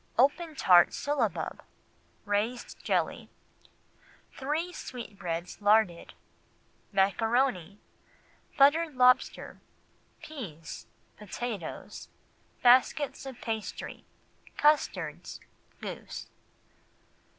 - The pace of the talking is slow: Yes, slow, 60 wpm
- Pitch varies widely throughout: Yes, wide, 5.7 semitones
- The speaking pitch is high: Yes, high, 240 Hz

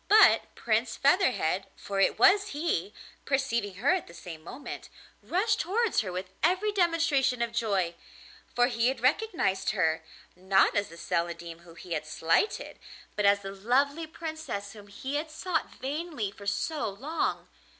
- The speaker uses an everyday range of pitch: No, wide, 8.6 semitones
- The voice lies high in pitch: Yes, high, 235 Hz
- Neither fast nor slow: Yes, average, 160 wpm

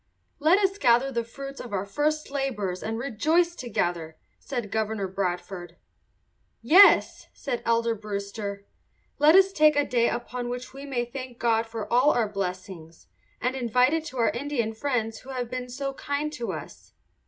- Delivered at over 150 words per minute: Yes, average, 165 wpm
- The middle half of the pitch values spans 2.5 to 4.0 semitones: No, average, 4.6 semitones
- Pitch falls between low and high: No, high, 240 Hz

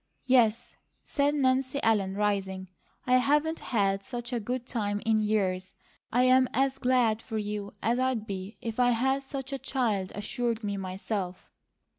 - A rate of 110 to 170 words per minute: Yes, average, 155 wpm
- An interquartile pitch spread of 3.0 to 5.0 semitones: Yes, average, 4.0 semitones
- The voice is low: No, high, 230 Hz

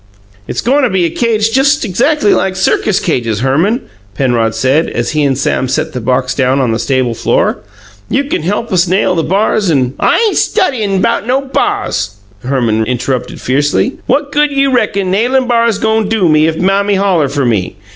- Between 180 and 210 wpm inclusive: Yes, average, 195 wpm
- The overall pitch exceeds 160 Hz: Yes, medium, 185 Hz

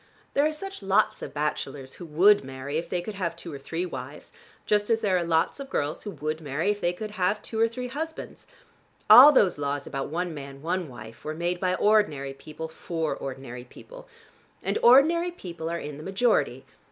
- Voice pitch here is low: No, medium, 170 Hz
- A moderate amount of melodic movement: No, wide, 6.3 semitones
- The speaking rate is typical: No, fast, 210 wpm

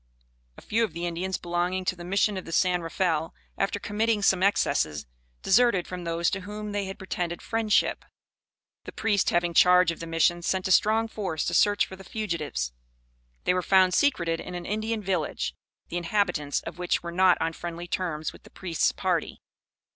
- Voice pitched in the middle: Yes, medium, 180 Hz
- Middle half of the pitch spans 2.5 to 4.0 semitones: Yes, average, 2.9 semitones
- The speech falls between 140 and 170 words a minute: No, average, 190 wpm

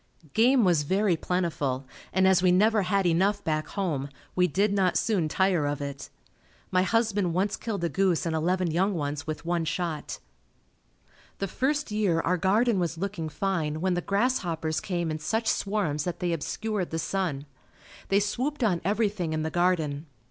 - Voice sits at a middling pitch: Yes, medium, 180 Hz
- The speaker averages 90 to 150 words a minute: No, average, 175 wpm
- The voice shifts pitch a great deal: No, average, 3.9 semitones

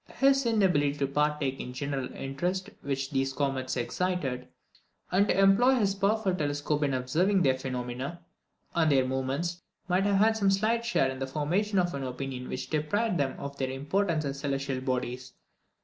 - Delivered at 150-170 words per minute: No, average, 180 wpm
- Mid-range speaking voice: Yes, medium, 145 Hz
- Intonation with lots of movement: Yes, wide, 6.4 semitones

